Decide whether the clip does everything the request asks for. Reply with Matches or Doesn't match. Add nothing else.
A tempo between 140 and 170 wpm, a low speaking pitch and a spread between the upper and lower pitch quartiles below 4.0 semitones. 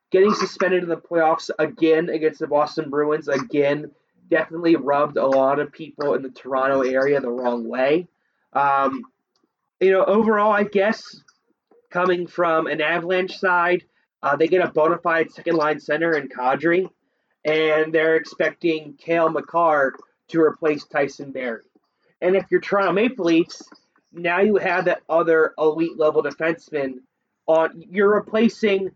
Doesn't match